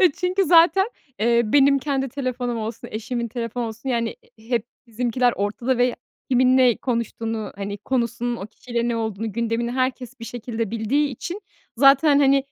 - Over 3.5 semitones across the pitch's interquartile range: No, narrow, 2.6 semitones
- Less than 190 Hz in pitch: No, high, 240 Hz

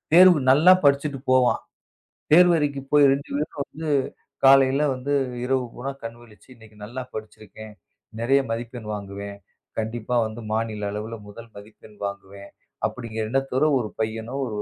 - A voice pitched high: No, low, 120 Hz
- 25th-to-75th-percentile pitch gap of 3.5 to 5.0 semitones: Yes, average, 4.0 semitones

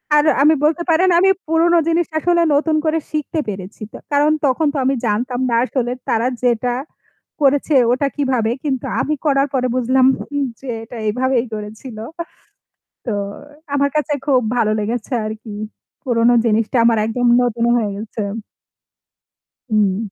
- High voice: Yes, very high, 255 Hz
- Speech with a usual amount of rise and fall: Yes, average, 4.4 semitones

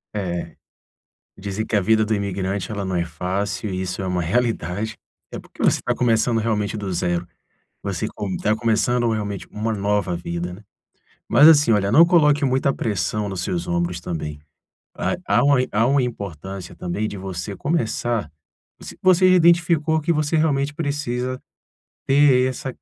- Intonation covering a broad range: Yes, wide, 5.7 semitones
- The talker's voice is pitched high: No, low, 105 Hz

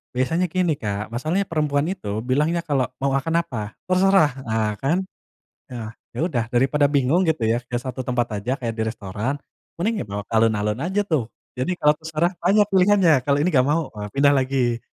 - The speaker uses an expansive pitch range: Yes, wide, 6.1 semitones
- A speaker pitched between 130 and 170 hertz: Yes, low, 135 Hz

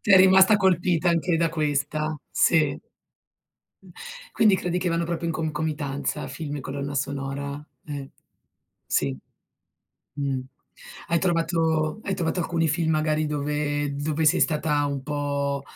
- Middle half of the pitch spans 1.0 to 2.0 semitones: No, average, 2.7 semitones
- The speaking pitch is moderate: Yes, medium, 155 Hz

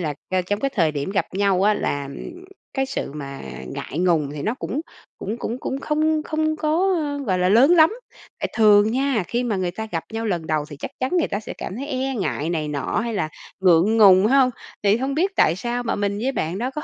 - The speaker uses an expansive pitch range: Yes, wide, 7.2 semitones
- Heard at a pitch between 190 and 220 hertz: Yes, high, 210 Hz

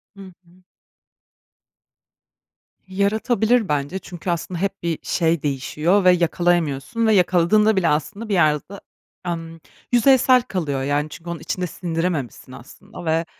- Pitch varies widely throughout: No, average, 3.7 semitones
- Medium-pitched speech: Yes, medium, 175 Hz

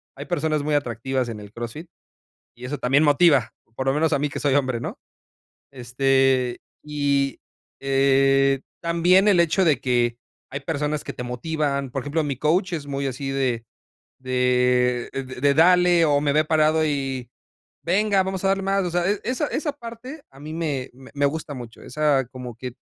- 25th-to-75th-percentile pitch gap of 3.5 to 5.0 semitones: Yes, average, 3.8 semitones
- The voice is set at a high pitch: No, medium, 140 Hz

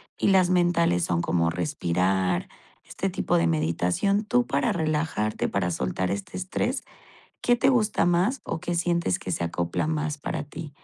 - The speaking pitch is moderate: Yes, medium, 150 Hz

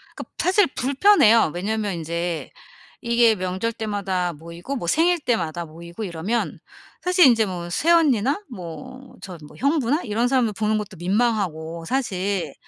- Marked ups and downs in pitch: Yes, wide, 6.5 semitones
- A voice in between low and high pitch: No, high, 215 Hz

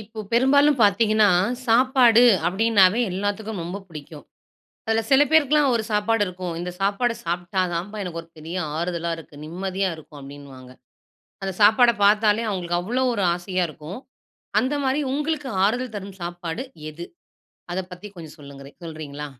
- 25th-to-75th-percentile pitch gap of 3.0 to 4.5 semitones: No, average, 4.9 semitones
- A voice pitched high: Yes, high, 195 Hz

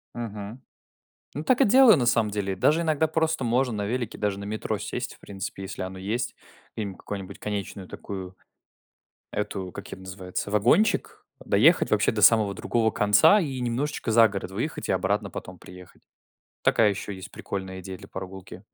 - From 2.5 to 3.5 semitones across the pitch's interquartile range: No, average, 4.0 semitones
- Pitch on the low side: Yes, low, 105 Hz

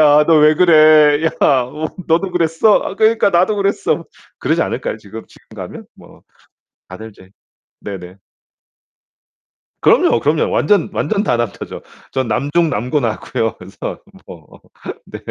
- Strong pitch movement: Yes, wide, 7.4 semitones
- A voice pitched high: No, medium, 150 Hz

